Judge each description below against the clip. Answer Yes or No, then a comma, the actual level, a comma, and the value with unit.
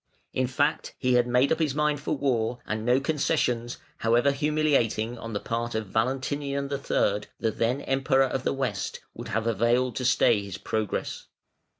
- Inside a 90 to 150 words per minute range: No, average, 175 wpm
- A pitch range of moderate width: Yes, average, 3.4 semitones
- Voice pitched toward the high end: No, low, 125 Hz